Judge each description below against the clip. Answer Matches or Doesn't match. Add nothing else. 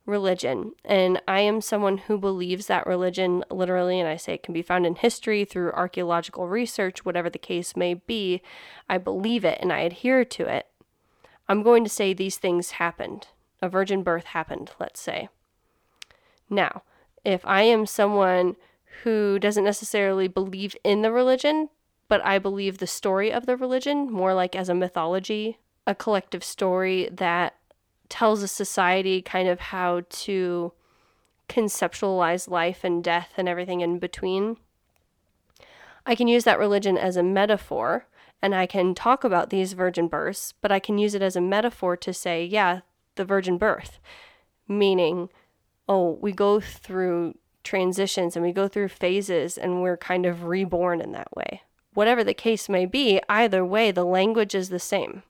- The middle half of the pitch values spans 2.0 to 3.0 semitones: Matches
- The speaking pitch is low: Doesn't match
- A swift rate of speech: Doesn't match